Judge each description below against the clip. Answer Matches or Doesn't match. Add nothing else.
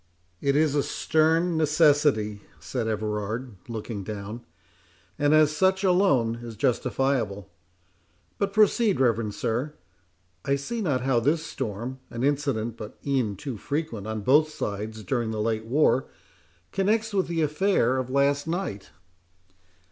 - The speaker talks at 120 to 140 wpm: Matches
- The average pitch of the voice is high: Doesn't match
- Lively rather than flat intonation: Matches